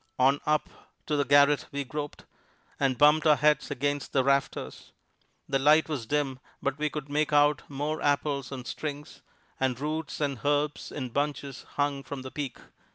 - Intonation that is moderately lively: No, narrow, 1.4 semitones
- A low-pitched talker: No, medium, 145 Hz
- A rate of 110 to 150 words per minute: No, average, 170 wpm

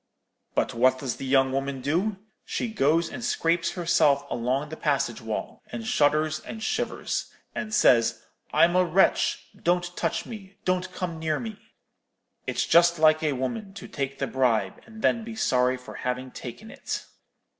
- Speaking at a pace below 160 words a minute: No, average, 165 wpm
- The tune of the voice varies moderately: No, wide, 5.7 semitones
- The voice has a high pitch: No, medium, 155 Hz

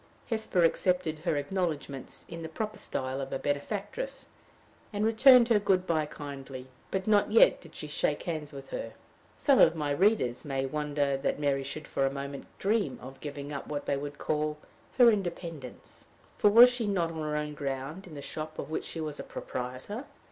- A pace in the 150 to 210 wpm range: Yes, average, 190 wpm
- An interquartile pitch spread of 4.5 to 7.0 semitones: Yes, wide, 5.5 semitones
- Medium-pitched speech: Yes, medium, 155 Hz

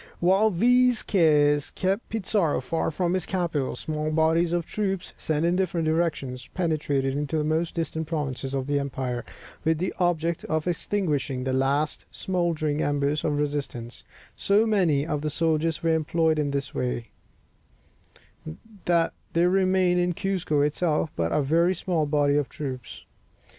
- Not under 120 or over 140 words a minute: No, average, 155 wpm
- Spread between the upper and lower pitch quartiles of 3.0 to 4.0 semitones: Yes, average, 3.3 semitones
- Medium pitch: Yes, medium, 160 Hz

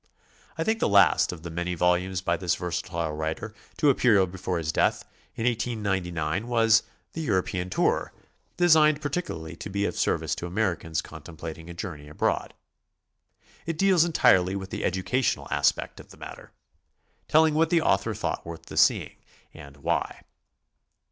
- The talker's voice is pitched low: Yes, very low, 95 Hz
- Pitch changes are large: Yes, wide, 6.3 semitones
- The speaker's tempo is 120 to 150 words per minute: No, average, 160 wpm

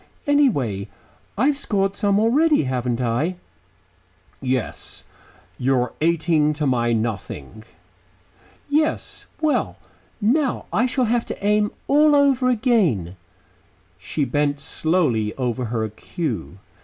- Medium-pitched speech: Yes, medium, 160 Hz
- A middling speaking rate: No, slow, 110 wpm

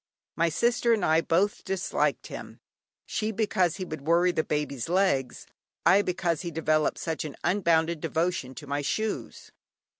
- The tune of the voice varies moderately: Yes, average, 3.5 semitones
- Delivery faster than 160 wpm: No, average, 155 wpm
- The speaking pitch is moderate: Yes, medium, 170 Hz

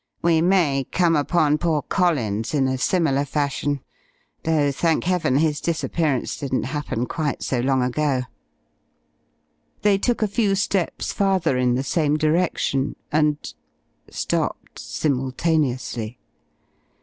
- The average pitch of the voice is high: No, medium, 150 Hz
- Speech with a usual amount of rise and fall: Yes, average, 4.1 semitones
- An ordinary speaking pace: No, slow, 120 wpm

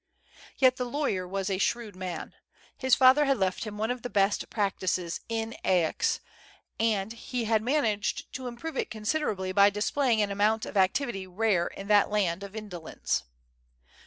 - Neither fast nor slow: Yes, average, 165 wpm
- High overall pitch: Yes, high, 210 Hz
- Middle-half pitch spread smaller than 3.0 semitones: No, average, 3.8 semitones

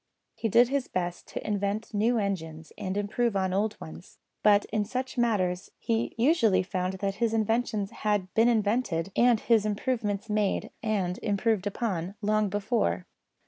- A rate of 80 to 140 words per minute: No, average, 155 wpm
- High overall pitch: Yes, high, 210 Hz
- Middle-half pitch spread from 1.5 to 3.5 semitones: Yes, average, 3.0 semitones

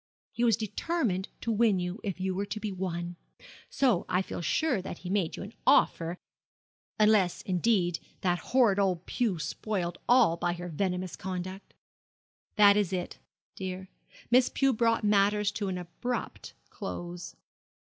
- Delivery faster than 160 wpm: No, average, 155 wpm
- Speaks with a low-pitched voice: No, high, 190 Hz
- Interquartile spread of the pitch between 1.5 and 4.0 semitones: Yes, average, 3.3 semitones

